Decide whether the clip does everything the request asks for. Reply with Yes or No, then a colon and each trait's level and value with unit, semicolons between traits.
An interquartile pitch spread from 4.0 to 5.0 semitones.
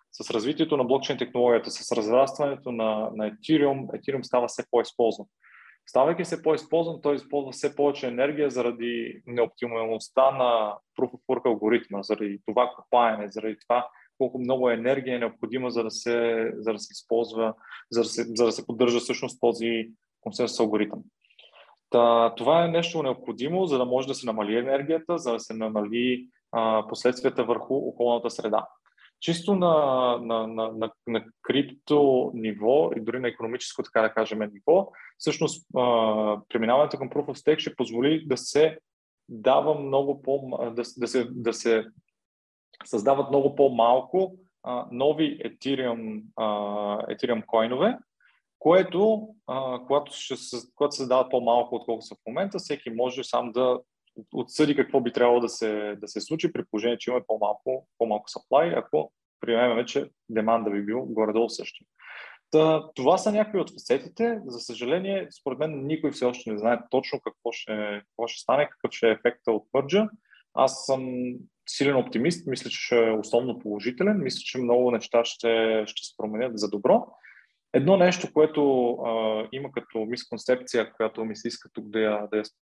No: average, 3.5 semitones